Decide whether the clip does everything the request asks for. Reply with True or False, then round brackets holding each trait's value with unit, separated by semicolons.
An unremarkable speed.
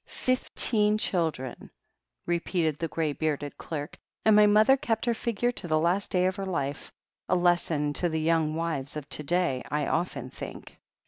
True (175 wpm)